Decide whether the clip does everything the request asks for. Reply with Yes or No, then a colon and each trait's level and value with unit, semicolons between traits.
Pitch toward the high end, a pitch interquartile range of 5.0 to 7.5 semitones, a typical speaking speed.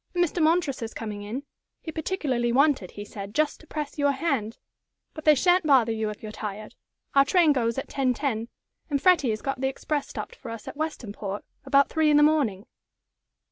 Yes: very high, 275 Hz; wide, 5.5 semitones; average, 195 wpm